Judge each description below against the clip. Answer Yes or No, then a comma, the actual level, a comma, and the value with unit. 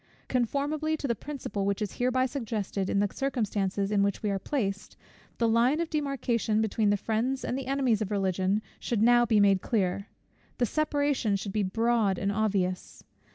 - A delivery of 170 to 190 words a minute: Yes, average, 180 wpm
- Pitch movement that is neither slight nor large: Yes, average, 4.4 semitones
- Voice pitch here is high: Yes, high, 220 Hz